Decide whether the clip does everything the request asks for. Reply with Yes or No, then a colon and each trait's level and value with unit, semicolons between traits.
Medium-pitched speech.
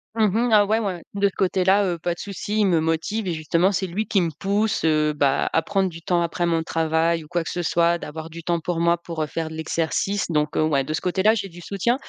Yes: medium, 170 Hz